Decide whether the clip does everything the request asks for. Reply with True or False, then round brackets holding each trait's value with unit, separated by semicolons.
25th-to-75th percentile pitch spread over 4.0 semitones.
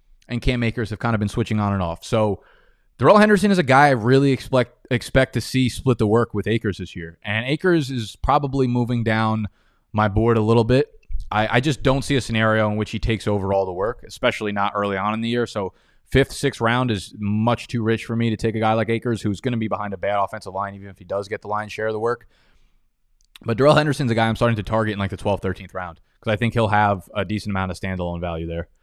False (3.1 semitones)